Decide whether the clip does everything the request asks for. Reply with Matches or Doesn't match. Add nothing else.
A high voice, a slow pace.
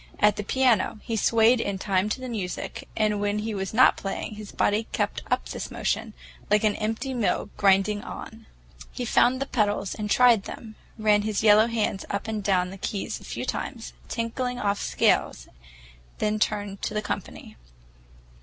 Doesn't match